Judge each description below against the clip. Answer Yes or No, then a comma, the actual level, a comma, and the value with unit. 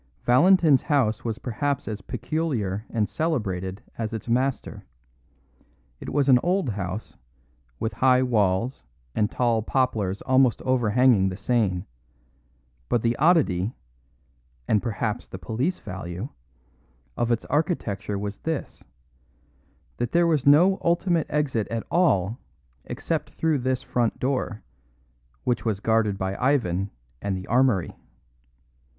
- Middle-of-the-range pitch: No, low, 120 Hz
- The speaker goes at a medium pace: No, slow, 125 wpm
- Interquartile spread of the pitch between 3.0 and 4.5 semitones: No, average, 5.0 semitones